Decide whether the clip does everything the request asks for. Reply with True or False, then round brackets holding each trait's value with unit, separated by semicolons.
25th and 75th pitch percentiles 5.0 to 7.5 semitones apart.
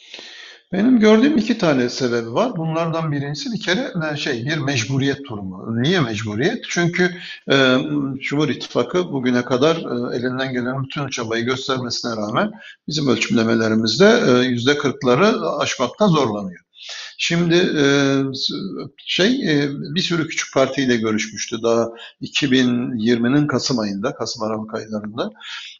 True (5.3 semitones)